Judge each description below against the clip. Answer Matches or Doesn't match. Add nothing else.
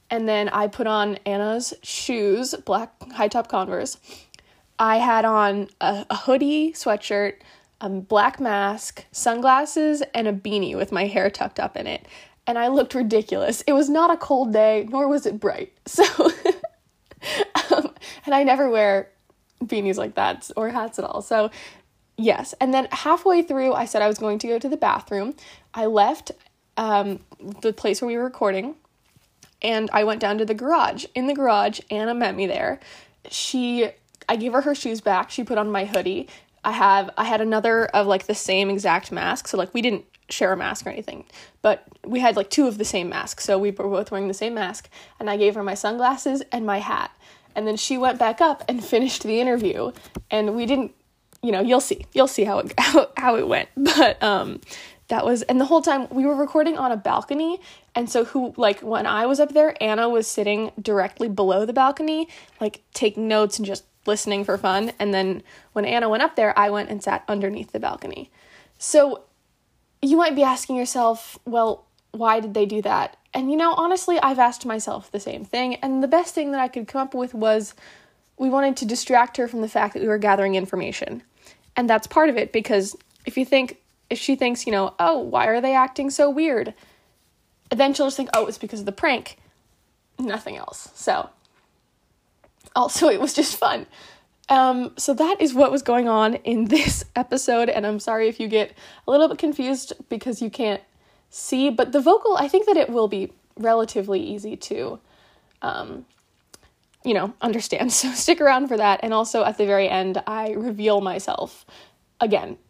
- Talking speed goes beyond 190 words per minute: Matches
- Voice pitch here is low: Doesn't match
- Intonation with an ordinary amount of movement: Matches